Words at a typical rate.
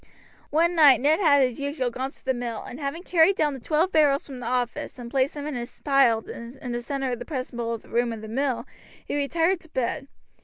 No: fast, 230 wpm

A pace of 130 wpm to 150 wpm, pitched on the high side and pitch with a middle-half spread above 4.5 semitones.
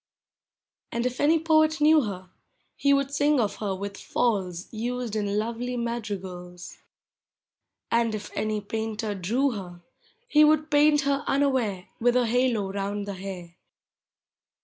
Yes: average, 140 wpm; high, 225 Hz; wide, 5.6 semitones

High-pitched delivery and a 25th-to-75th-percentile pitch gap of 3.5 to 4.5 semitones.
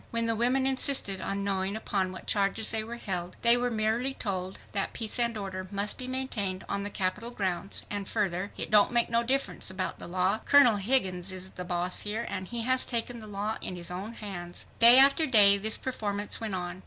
Yes: high, 205 Hz; average, 3.8 semitones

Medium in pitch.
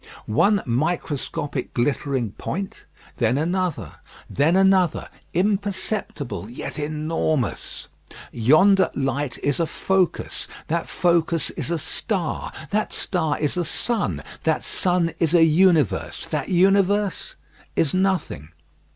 Yes: medium, 165 Hz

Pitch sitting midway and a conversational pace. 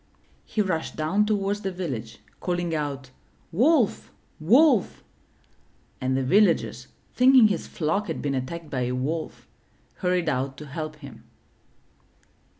No: medium, 165 Hz; slow, 130 wpm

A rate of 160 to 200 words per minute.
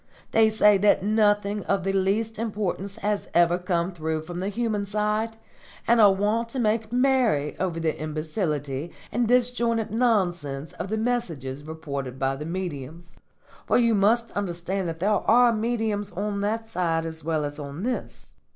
Yes: average, 165 wpm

